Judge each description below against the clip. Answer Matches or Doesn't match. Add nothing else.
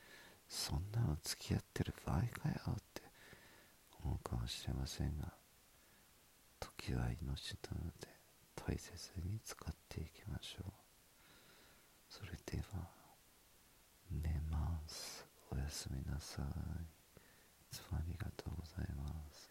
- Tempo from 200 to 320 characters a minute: Matches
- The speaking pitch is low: Matches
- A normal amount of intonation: Matches